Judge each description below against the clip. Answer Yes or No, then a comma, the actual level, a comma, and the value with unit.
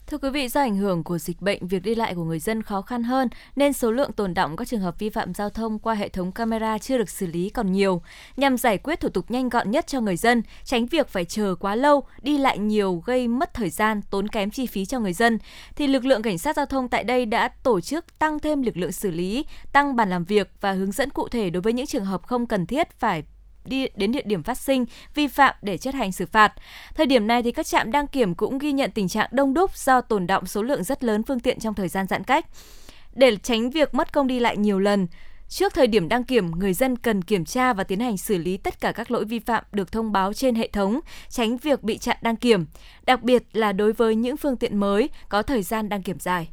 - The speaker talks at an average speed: No, fast, 265 wpm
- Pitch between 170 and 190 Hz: No, high, 230 Hz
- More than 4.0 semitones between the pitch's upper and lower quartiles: Yes, average, 4.5 semitones